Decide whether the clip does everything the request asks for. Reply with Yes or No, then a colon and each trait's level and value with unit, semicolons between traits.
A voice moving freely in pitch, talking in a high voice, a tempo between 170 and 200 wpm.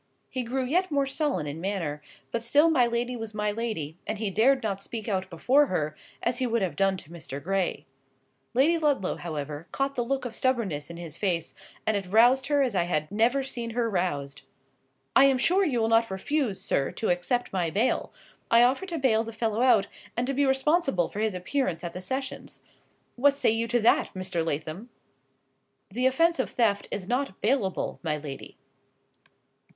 Yes: wide, 6.3 semitones; high, 225 Hz; average, 195 wpm